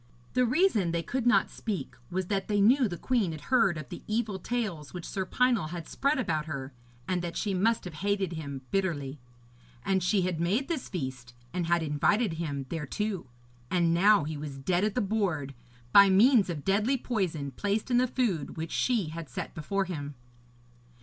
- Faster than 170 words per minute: Yes, average, 190 wpm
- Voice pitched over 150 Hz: Yes, medium, 185 Hz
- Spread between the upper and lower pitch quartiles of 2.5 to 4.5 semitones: No, wide, 5.4 semitones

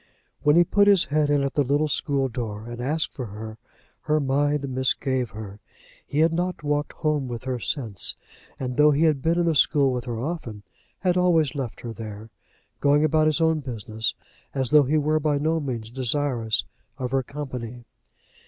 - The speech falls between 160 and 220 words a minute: Yes, average, 190 wpm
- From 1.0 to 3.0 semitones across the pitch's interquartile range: No, average, 4.1 semitones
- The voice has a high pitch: No, medium, 140 Hz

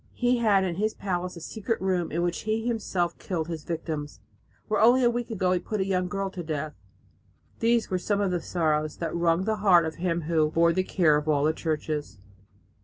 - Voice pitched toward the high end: No, medium, 180 Hz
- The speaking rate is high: Yes, fast, 220 wpm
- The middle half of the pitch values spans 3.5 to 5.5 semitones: Yes, average, 3.9 semitones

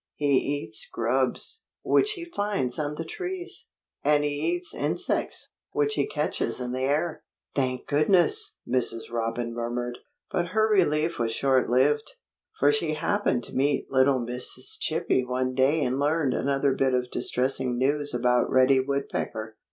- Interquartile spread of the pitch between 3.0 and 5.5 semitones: Yes, average, 3.8 semitones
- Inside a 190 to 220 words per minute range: No, average, 150 wpm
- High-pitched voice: No, medium, 140 Hz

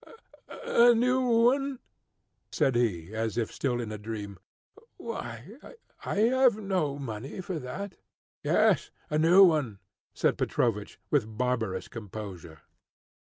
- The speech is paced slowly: Yes, slow, 120 wpm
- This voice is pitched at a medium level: No, low, 125 Hz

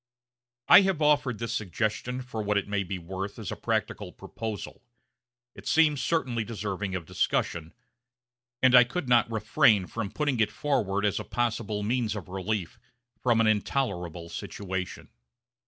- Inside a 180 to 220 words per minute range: No, average, 155 wpm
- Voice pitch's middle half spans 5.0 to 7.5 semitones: No, average, 4.2 semitones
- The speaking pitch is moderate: No, low, 110 Hz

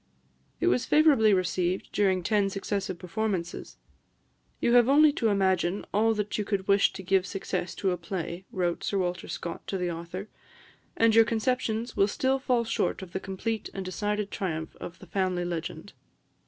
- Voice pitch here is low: No, high, 195 Hz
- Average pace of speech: Yes, average, 175 wpm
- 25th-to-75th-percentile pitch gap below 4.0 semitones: Yes, average, 3.4 semitones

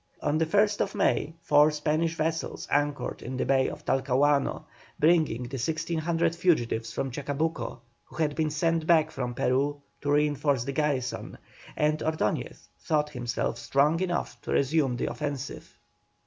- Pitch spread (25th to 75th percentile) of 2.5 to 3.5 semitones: Yes, average, 3.1 semitones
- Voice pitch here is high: No, medium, 150 Hz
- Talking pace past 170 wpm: No, average, 150 wpm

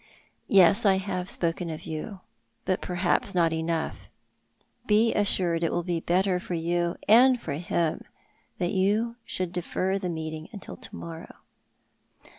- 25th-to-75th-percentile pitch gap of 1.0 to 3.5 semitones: Yes, average, 2.8 semitones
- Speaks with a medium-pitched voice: Yes, medium, 180 Hz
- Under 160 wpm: Yes, average, 150 wpm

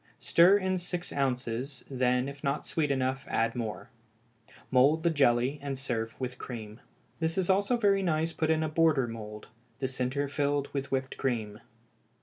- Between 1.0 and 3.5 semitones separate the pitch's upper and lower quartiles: No, average, 4.2 semitones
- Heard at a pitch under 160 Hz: Yes, medium, 140 Hz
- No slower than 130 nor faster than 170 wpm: Yes, average, 165 wpm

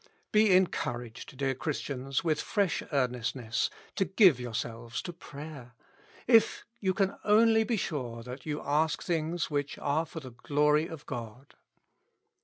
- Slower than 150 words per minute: Yes, average, 140 wpm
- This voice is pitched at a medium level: Yes, medium, 150 Hz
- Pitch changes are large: Yes, wide, 5.8 semitones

